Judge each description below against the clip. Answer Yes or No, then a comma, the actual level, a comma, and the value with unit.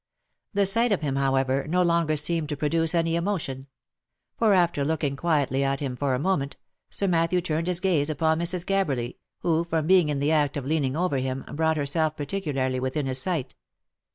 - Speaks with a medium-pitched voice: Yes, medium, 155 Hz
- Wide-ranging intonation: No, average, 3.8 semitones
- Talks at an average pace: Yes, average, 190 wpm